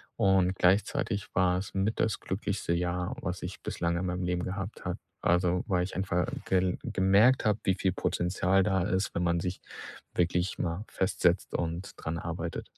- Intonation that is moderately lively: No, narrow, 1.5 semitones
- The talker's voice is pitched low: Yes, very low, 90 Hz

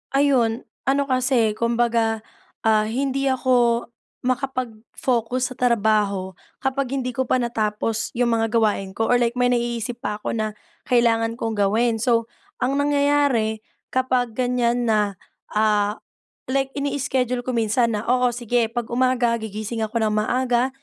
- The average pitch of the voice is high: Yes, high, 235 Hz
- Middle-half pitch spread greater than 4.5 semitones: No, narrow, 2.4 semitones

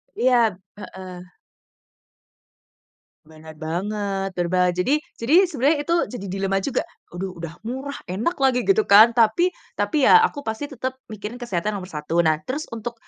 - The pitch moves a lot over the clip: Yes, wide, 6.3 semitones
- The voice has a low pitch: No, high, 215 Hz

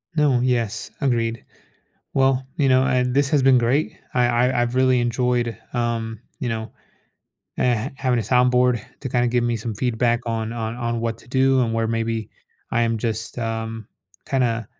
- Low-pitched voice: Yes, low, 120 Hz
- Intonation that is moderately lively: No, narrow, 1.9 semitones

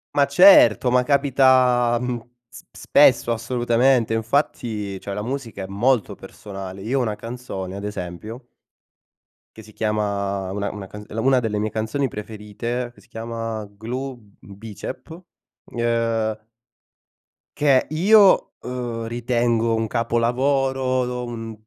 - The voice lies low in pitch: Yes, low, 115 Hz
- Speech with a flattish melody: No, average, 3.0 semitones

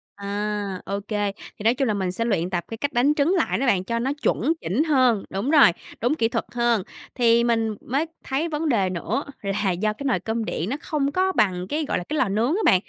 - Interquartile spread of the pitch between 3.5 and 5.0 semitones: No, wide, 5.6 semitones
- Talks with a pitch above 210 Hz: Yes, high, 230 Hz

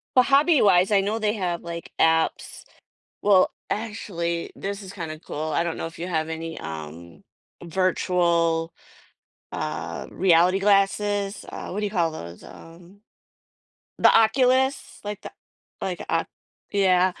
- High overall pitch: No, medium, 180 Hz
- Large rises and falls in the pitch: No, average, 3.8 semitones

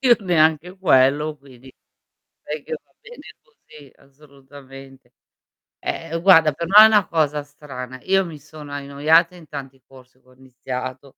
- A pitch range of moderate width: Yes, average, 3.7 semitones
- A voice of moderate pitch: Yes, medium, 145 Hz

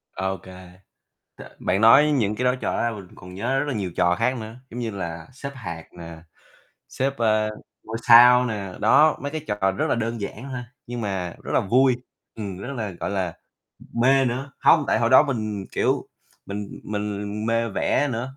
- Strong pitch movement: No, average, 4.4 semitones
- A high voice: No, low, 110 Hz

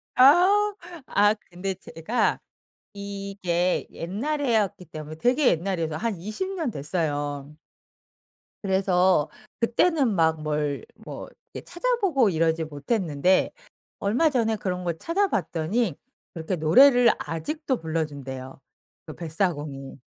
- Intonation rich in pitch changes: Yes, wide, 7.1 semitones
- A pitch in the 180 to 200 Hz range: Yes, medium, 185 Hz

